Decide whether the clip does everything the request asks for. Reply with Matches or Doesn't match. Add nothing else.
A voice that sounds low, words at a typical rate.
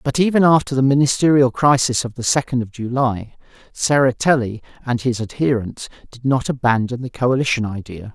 Matches